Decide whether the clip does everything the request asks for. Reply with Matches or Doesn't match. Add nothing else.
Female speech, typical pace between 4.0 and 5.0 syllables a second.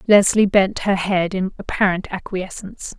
Matches